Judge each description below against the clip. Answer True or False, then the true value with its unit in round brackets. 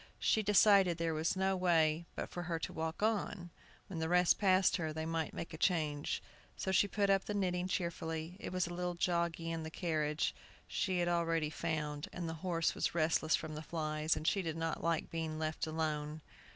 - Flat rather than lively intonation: True (2.2 semitones)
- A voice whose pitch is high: False (165 Hz)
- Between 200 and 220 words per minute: True (205 wpm)